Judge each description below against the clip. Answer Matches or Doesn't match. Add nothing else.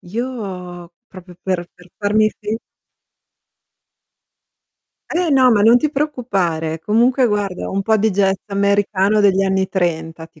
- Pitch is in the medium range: Doesn't match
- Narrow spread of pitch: Doesn't match